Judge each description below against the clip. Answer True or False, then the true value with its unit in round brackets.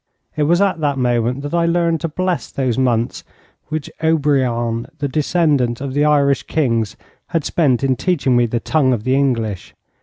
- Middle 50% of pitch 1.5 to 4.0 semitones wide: False (4.4 semitones)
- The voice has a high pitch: False (140 Hz)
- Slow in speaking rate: False (180 wpm)